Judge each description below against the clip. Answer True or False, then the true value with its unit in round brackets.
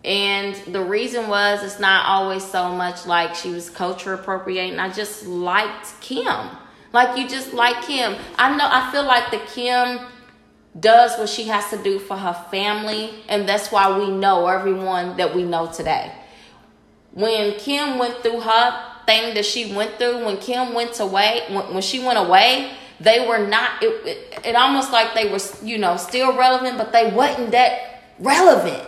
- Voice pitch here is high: True (215 Hz)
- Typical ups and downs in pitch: True (3.9 semitones)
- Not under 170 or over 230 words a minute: True (180 wpm)